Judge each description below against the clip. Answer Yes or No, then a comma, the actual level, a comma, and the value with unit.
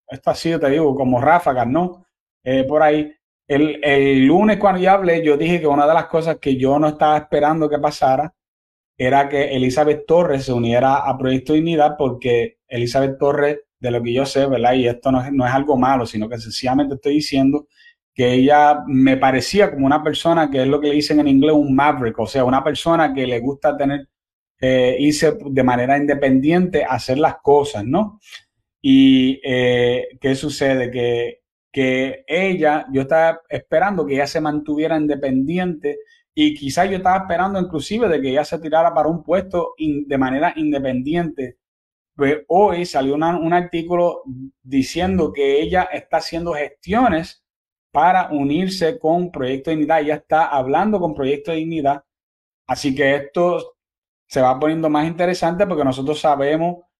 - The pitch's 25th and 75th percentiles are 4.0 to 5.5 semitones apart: No, average, 3.6 semitones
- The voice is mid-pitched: Yes, medium, 150 Hz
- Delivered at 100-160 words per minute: No, average, 175 wpm